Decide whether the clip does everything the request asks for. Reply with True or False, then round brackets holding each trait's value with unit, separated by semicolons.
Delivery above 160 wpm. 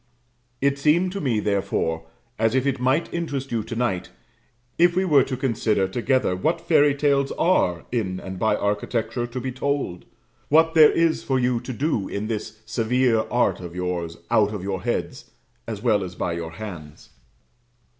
True (175 wpm)